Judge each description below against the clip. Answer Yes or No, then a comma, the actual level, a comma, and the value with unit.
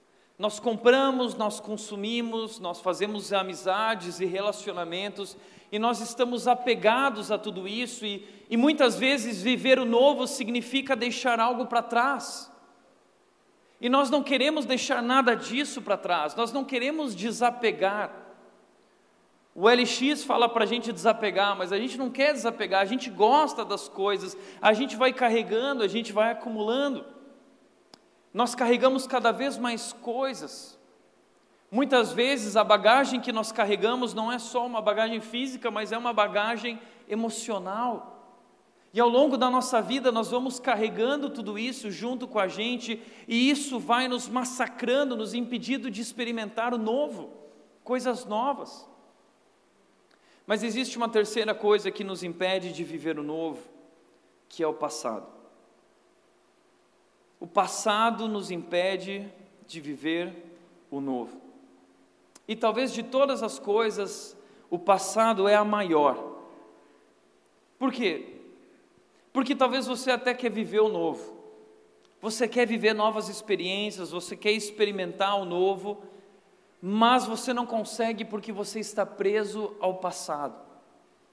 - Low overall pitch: No, high, 225 Hz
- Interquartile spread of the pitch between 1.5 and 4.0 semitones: Yes, average, 3.5 semitones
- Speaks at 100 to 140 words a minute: Yes, average, 135 wpm